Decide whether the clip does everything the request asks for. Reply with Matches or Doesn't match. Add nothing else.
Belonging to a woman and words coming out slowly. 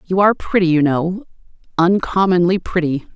Matches